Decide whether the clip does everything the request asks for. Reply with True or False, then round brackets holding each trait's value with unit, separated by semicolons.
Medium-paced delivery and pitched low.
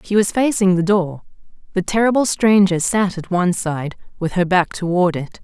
False (190 wpm; 185 Hz)